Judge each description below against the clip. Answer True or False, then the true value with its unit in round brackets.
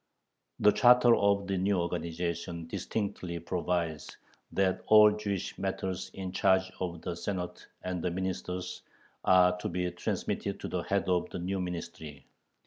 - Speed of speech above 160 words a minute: False (145 wpm)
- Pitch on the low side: True (90 Hz)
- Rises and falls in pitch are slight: True (1.9 semitones)